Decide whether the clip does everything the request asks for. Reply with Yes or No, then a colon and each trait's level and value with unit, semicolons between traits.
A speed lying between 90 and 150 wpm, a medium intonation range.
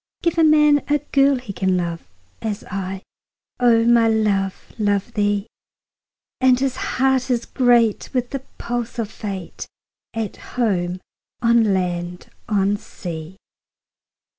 Yes: slow, 135 wpm; average, 4.3 semitones